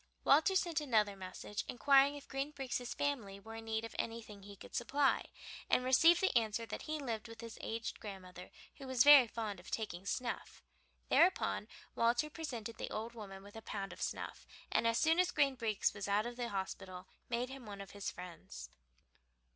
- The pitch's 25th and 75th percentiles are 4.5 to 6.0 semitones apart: Yes, average, 4.9 semitones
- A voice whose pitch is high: Yes, high, 230 Hz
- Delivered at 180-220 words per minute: Yes, average, 195 wpm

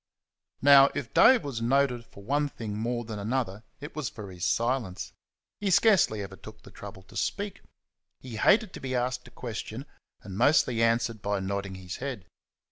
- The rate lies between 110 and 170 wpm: No, average, 180 wpm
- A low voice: Yes, low, 115 Hz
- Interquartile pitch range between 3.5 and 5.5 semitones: Yes, average, 5.1 semitones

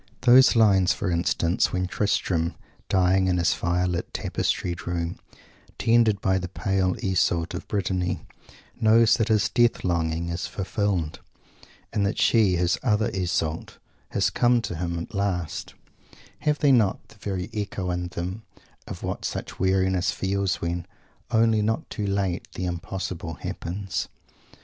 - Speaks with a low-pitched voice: Yes, very low, 95 Hz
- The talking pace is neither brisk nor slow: Yes, average, 145 wpm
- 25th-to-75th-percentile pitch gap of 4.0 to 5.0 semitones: No, average, 3.0 semitones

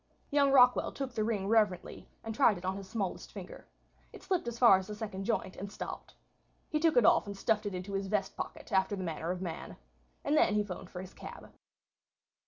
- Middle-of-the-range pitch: No, high, 205 Hz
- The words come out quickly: Yes, fast, 220 wpm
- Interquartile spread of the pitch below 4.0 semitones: Yes, average, 3.4 semitones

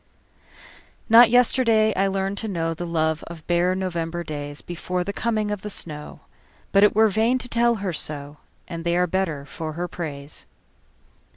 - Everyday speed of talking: Yes, average, 155 wpm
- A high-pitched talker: No, medium, 180 Hz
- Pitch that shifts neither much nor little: Yes, average, 4.3 semitones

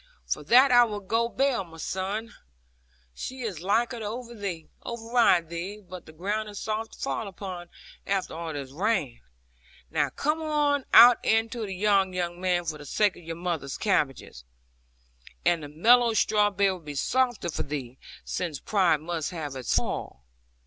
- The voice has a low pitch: No, high, 190 Hz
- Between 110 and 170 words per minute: Yes, average, 165 wpm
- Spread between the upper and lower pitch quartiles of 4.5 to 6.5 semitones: Yes, average, 5.2 semitones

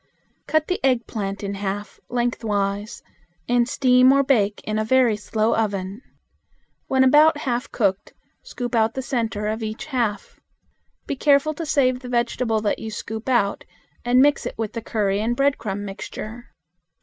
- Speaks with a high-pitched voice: Yes, high, 230 Hz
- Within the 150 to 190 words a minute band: Yes, average, 160 wpm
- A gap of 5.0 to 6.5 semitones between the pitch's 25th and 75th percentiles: No, average, 3.5 semitones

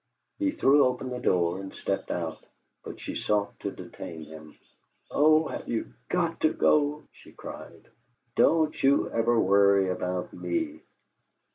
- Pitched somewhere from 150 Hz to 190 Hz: No, low, 115 Hz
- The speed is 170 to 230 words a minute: No, average, 145 wpm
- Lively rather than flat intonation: Yes, wide, 8.7 semitones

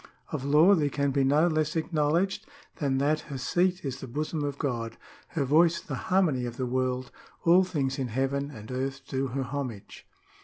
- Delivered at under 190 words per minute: No, average, 195 wpm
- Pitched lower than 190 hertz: Yes, medium, 140 Hz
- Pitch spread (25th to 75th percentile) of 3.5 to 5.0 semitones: No, average, 3.0 semitones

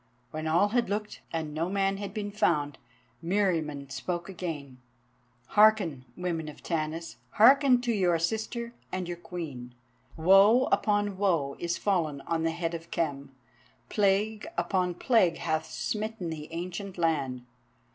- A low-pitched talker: No, medium, 175 Hz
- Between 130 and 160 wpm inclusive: Yes, average, 140 wpm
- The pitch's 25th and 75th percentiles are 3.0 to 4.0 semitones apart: No, average, 4.4 semitones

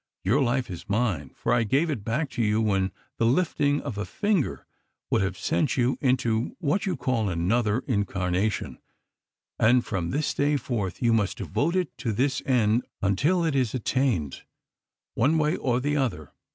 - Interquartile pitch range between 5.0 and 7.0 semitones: Yes, wide, 5.5 semitones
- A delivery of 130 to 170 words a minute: No, average, 180 wpm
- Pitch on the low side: Yes, low, 120 Hz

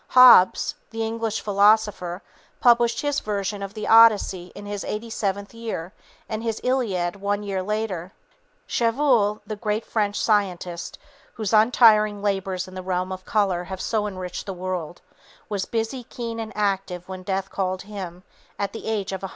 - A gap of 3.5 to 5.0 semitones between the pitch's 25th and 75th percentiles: No, average, 2.9 semitones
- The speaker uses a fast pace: No, average, 165 wpm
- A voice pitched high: Yes, high, 205 Hz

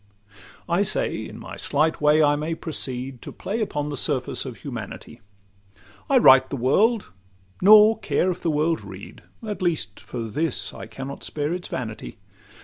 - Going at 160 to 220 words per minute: Yes, average, 165 wpm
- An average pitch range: Yes, average, 5.0 semitones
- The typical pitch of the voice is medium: Yes, medium, 150 Hz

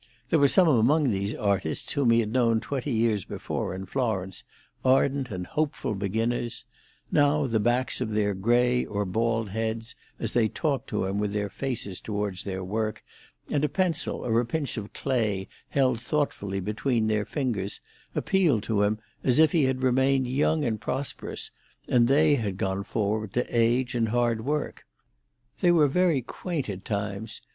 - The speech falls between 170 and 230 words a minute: Yes, average, 175 wpm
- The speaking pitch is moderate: No, low, 115 Hz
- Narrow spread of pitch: No, average, 4.6 semitones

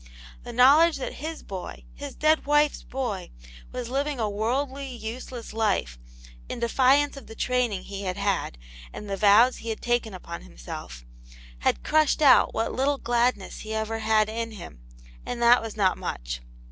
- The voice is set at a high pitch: Yes, high, 230 Hz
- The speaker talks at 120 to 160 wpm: No, average, 170 wpm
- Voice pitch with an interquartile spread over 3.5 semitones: Yes, average, 4.6 semitones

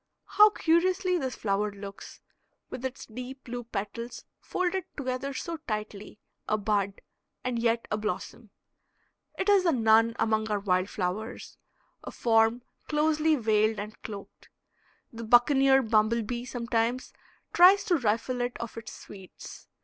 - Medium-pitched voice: No, high, 235 Hz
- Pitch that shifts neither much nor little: Yes, average, 3.9 semitones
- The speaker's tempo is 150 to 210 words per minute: No, average, 140 wpm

